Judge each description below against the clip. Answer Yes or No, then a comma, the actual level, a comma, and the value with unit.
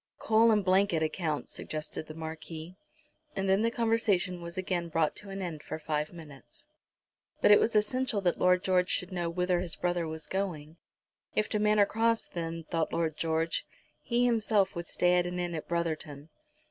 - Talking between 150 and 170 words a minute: No, average, 185 wpm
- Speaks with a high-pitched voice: No, medium, 175 Hz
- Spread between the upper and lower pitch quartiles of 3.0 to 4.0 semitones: Yes, average, 3.7 semitones